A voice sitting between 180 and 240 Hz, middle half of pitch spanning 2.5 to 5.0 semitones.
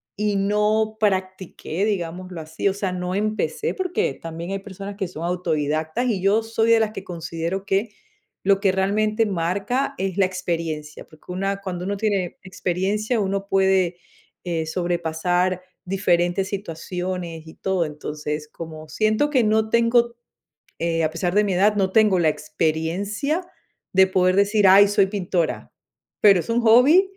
Yes: high, 190 Hz; average, 3.5 semitones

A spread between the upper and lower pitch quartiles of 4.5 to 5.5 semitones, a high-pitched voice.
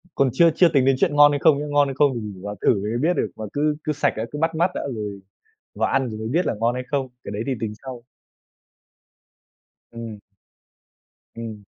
No: average, 4.9 semitones; low, 130 Hz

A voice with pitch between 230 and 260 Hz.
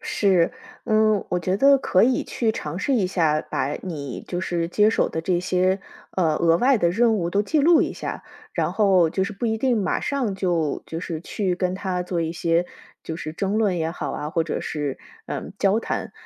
No: medium, 185 Hz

